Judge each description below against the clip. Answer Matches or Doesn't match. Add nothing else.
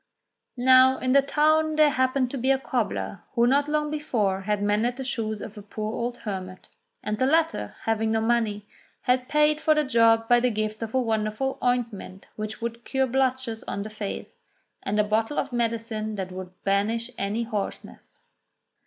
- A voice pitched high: Matches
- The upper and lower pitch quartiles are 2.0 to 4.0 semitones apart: Matches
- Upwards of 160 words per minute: Matches